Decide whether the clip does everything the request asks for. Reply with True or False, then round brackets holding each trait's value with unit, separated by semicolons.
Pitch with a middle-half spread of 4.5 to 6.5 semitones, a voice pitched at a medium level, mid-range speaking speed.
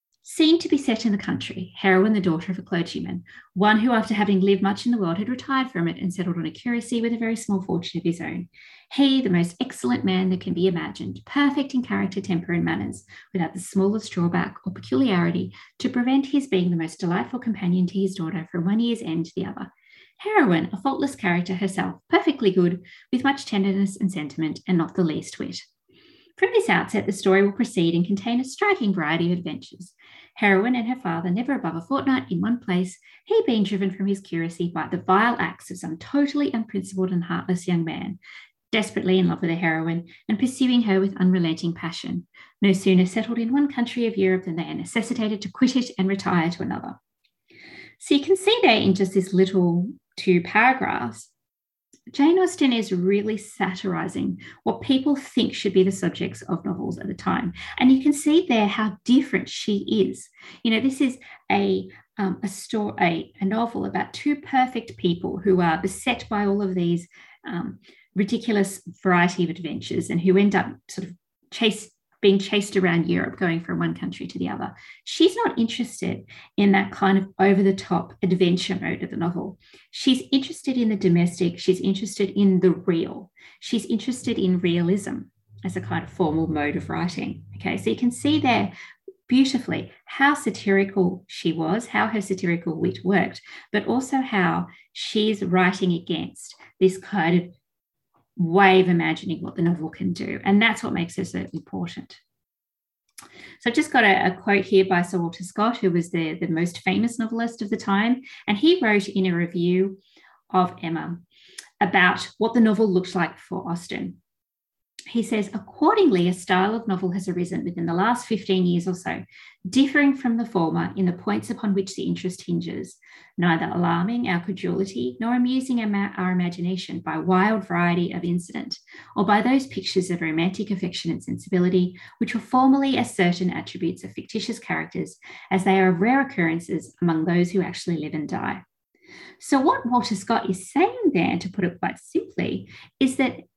False (4.8 semitones; 195 Hz; 190 wpm)